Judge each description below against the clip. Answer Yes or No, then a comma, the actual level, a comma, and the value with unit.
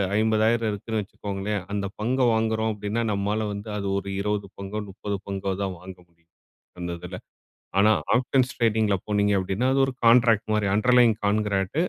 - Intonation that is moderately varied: No, narrow, 2.0 semitones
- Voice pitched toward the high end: No, low, 105 Hz